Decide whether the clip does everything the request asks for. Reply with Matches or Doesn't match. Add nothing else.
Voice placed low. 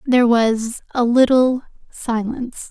Doesn't match